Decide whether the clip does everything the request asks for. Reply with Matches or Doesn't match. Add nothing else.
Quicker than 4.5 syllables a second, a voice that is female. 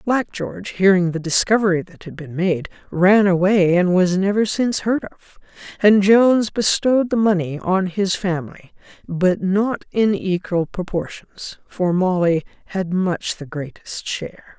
Doesn't match